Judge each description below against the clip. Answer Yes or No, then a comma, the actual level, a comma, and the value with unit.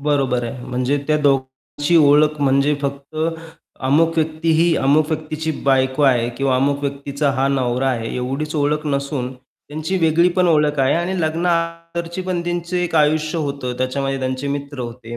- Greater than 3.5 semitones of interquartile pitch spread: No, average, 2.9 semitones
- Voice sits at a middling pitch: Yes, medium, 145 Hz